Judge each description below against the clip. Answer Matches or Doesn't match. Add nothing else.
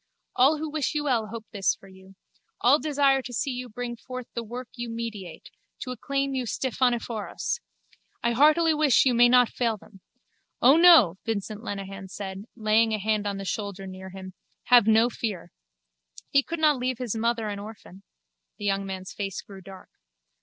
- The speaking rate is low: Doesn't match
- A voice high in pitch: Matches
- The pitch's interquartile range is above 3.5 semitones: Matches